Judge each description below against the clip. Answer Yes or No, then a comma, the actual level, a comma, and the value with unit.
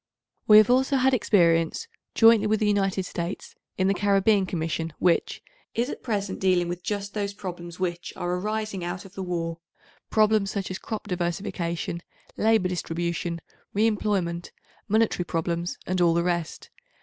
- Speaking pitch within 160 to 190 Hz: Yes, medium, 185 Hz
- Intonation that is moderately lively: Yes, average, 3.5 semitones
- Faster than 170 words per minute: No, average, 160 wpm